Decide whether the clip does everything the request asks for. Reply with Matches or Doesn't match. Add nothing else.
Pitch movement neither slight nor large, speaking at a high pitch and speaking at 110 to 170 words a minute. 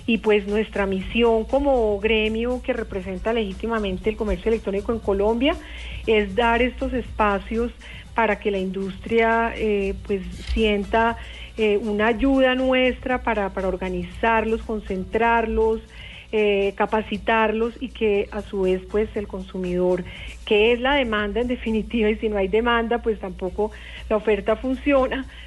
Doesn't match